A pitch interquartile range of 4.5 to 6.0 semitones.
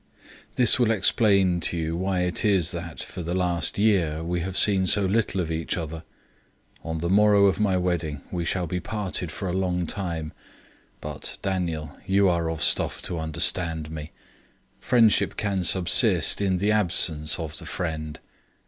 No: average, 3.0 semitones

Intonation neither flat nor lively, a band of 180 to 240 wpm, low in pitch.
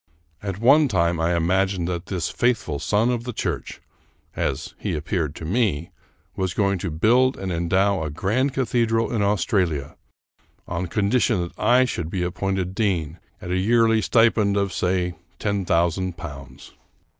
No: average, 4.4 semitones; average, 170 wpm; very low, 95 Hz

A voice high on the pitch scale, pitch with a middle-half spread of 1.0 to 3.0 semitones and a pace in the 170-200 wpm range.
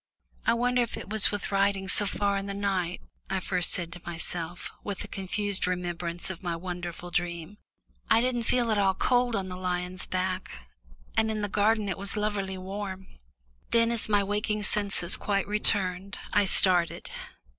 Yes: high, 195 Hz; narrow, 2.5 semitones; average, 175 wpm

